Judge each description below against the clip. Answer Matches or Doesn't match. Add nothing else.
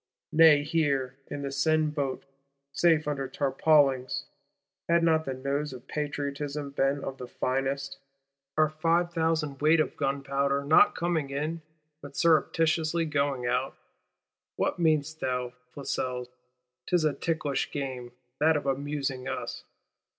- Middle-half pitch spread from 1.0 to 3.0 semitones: Matches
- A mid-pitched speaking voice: Matches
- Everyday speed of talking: Doesn't match